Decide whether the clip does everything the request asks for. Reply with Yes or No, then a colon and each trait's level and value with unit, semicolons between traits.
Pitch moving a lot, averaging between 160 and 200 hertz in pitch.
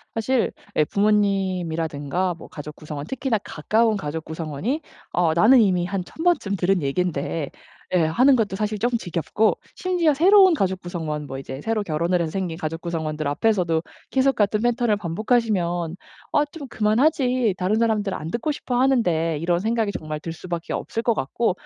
Yes: wide, 5.9 semitones; high, 190 Hz